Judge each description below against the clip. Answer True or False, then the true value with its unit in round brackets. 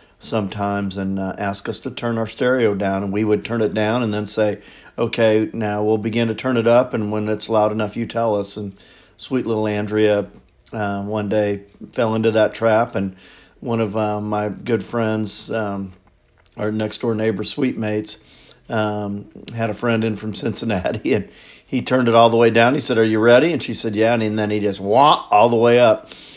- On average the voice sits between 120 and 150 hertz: False (110 Hz)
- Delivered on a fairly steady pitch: True (1.8 semitones)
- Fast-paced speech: True (210 wpm)